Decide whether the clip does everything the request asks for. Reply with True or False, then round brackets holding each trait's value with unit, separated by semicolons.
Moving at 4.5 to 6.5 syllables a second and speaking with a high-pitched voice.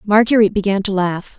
True (6.2 syllables/s; 200 Hz)